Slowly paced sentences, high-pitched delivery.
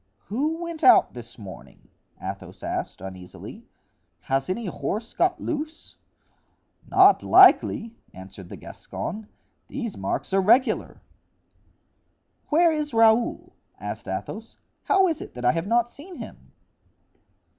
Yes: slow, 125 wpm; high, 225 Hz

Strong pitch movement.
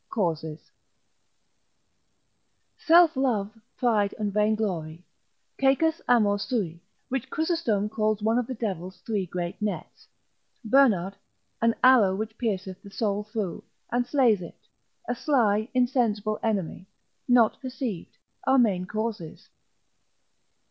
No: average, 3.9 semitones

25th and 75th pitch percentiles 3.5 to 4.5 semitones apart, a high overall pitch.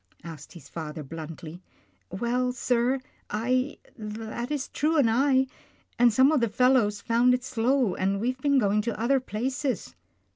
Yes: average, 4.1 semitones; high, 235 Hz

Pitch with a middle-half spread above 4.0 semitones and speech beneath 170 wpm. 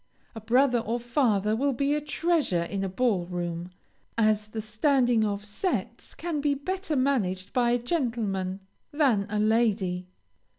Yes: wide, 5.6 semitones; average, 155 wpm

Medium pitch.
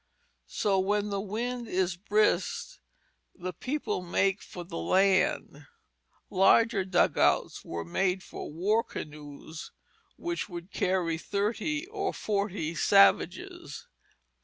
No: high, 195 Hz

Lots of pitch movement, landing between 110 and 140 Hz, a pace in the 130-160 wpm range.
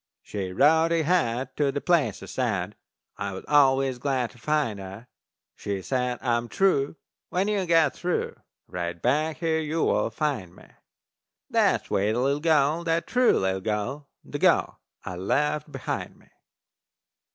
Yes: wide, 6.1 semitones; low, 135 Hz; average, 155 wpm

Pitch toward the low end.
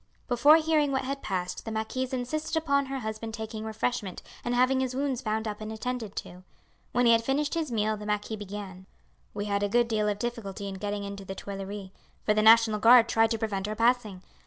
No: high, 220 Hz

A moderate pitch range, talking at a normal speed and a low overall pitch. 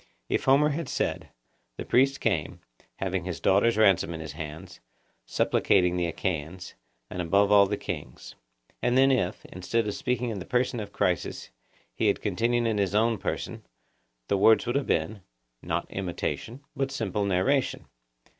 Yes: average, 5.0 semitones; average, 165 wpm; low, 100 Hz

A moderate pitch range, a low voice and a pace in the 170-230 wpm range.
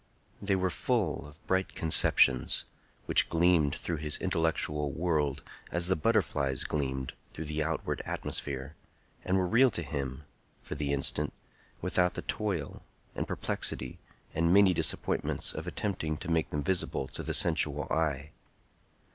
No: average, 3.8 semitones; very low, 80 Hz; average, 145 wpm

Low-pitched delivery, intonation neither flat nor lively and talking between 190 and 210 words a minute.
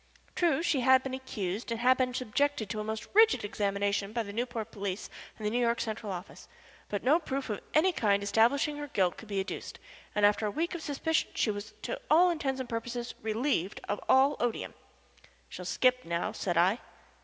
No: high, 230 Hz; average, 4.7 semitones; average, 200 wpm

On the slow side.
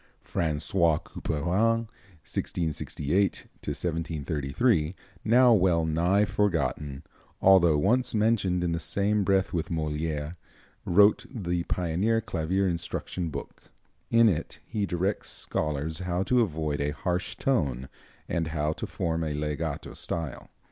Yes: slow, 120 wpm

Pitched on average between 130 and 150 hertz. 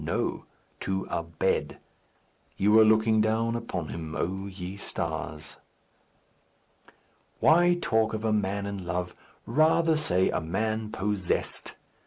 No: low, 100 Hz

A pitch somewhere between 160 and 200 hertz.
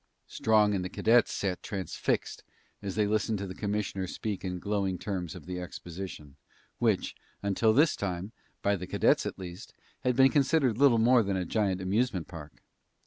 No: low, 100 Hz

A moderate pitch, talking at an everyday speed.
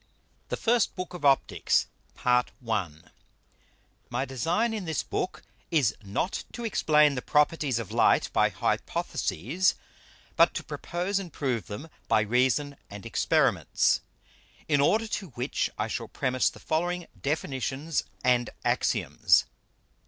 No: medium, 145 Hz; slow, 130 wpm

